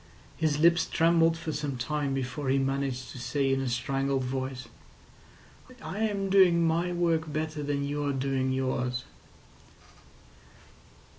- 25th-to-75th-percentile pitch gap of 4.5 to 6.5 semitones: No, average, 3.6 semitones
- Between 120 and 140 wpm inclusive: Yes, slow, 135 wpm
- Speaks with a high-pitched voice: No, medium, 140 Hz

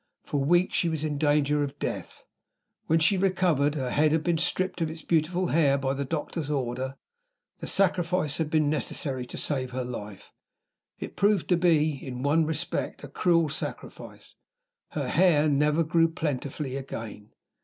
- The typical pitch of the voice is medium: Yes, medium, 150 Hz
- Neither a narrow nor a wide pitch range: Yes, average, 3.3 semitones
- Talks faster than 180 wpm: No, average, 165 wpm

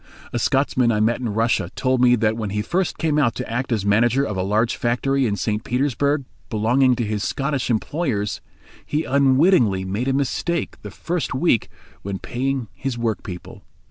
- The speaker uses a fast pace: No, average, 180 wpm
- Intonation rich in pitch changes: No, average, 4.2 semitones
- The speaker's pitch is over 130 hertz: No, low, 120 Hz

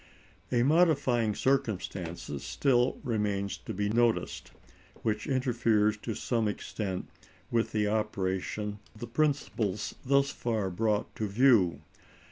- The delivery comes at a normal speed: No, slow, 115 wpm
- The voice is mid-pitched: No, low, 110 Hz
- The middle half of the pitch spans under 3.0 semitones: No, average, 3.3 semitones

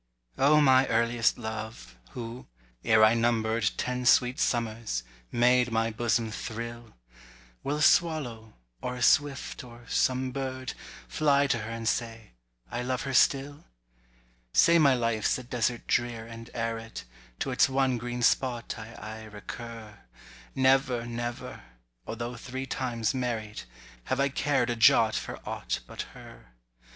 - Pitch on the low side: Yes, low, 120 Hz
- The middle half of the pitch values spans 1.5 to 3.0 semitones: Yes, narrow, 2.4 semitones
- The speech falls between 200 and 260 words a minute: No, average, 140 wpm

